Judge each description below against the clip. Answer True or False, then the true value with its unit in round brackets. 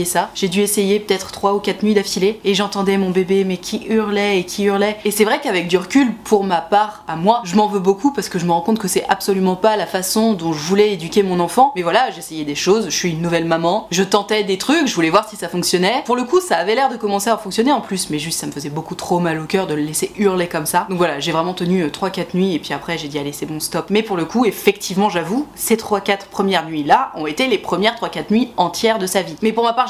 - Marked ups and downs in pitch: False (3.5 semitones)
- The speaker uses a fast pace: True (285 wpm)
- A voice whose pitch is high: True (195 Hz)